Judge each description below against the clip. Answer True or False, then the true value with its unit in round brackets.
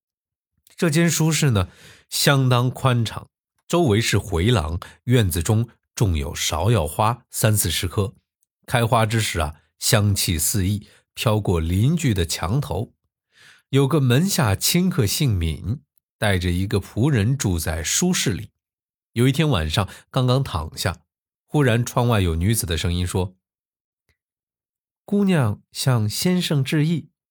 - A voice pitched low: True (110 Hz)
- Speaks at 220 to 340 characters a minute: False (195 characters per minute)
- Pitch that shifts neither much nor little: False (6.2 semitones)